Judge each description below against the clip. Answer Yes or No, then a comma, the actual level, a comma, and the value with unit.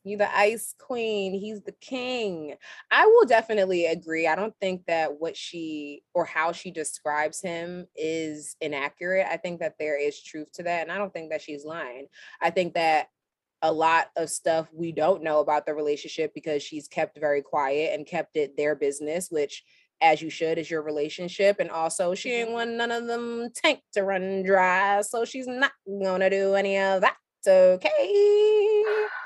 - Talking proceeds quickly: No, average, 185 wpm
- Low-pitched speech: No, medium, 180 Hz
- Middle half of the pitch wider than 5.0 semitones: Yes, wide, 5.4 semitones